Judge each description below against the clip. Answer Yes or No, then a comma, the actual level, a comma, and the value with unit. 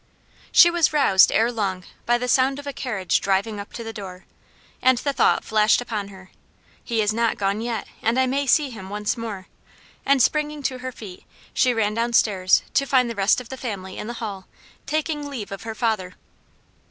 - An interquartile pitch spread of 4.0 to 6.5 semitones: Yes, average, 4.3 semitones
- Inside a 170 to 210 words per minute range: Yes, average, 200 wpm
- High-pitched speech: Yes, high, 230 Hz